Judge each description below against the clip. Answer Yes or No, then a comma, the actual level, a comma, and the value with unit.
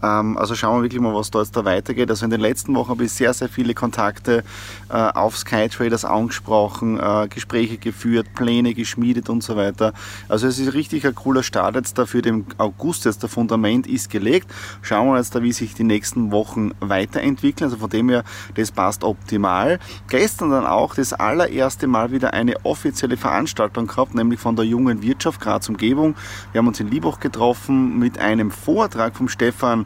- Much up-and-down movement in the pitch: No, narrow, 2.4 semitones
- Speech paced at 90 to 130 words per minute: No, fast, 190 wpm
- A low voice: Yes, low, 115 Hz